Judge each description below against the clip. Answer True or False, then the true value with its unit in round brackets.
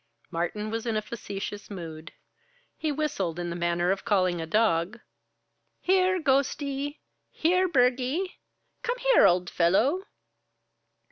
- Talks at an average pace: False (125 wpm)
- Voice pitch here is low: False (225 Hz)